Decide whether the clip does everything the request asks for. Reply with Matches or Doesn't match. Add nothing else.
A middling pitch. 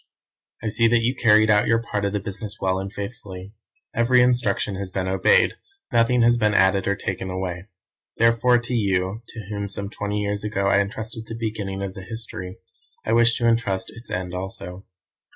Doesn't match